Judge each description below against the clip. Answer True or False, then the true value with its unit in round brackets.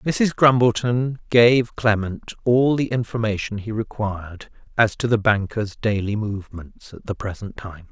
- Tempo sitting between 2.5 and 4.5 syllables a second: True (4.4 syllables/s)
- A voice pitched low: True (110 Hz)